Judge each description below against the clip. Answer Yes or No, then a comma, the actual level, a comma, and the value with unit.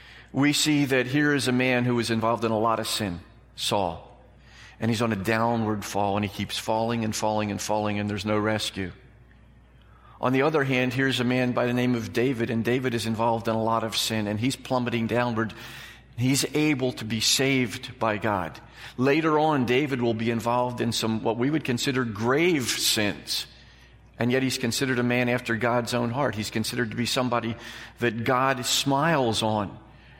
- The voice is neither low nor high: No, low, 120 Hz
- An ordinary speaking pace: Yes, average, 195 wpm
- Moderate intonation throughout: No, narrow, 2.2 semitones